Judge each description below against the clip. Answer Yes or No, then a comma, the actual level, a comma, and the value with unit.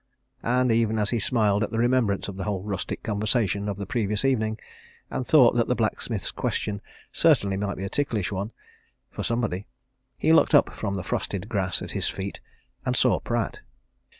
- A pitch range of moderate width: Yes, average, 3.0 semitones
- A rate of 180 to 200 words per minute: Yes, average, 185 wpm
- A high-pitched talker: No, low, 105 Hz